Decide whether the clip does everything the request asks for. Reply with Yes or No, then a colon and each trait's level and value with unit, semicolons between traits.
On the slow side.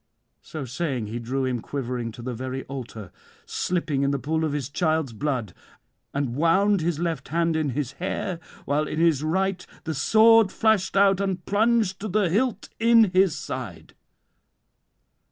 No: average, 165 wpm